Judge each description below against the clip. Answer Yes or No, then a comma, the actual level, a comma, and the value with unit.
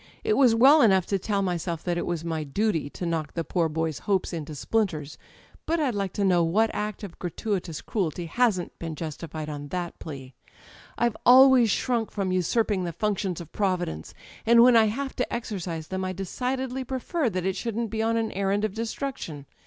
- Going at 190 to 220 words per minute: Yes, average, 200 wpm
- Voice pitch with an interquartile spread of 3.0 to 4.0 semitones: No, average, 5.3 semitones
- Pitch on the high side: Yes, high, 195 Hz